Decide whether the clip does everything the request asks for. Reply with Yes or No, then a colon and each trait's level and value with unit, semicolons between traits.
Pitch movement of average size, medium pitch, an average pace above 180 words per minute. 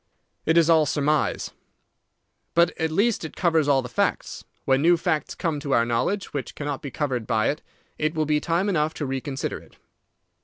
Yes: average, 3.0 semitones; medium, 150 Hz; average, 190 wpm